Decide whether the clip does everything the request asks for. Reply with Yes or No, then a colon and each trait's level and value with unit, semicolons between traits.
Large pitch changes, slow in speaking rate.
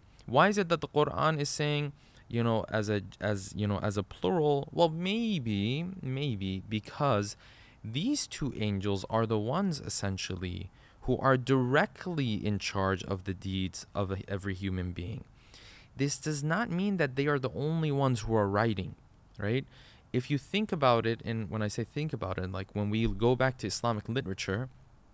No: wide, 5.9 semitones; average, 180 wpm